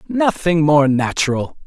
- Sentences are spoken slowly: Yes, slow, 110 wpm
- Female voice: No, male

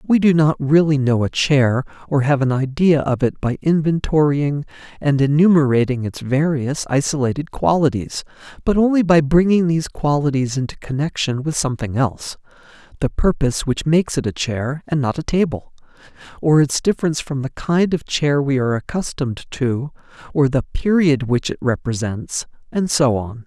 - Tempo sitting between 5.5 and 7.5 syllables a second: No, 5.1 syllables/s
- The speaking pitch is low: No, medium, 145 Hz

